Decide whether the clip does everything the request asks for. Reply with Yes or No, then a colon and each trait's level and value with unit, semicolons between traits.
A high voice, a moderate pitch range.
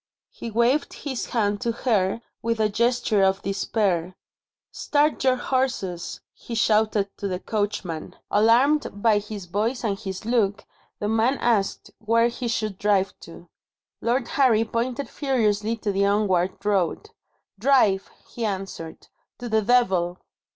Yes: high, 215 Hz; average, 3.2 semitones